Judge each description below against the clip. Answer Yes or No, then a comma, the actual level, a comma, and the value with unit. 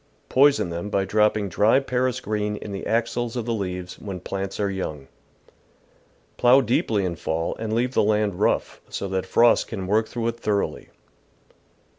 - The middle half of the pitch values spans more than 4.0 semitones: No, average, 3.3 semitones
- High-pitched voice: No, low, 105 Hz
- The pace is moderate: Yes, average, 170 wpm